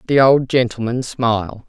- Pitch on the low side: Yes, low, 120 Hz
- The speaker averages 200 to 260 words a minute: No, average, 145 wpm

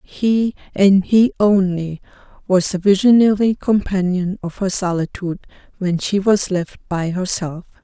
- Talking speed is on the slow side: Yes, slow, 130 wpm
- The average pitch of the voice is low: No, high, 190 Hz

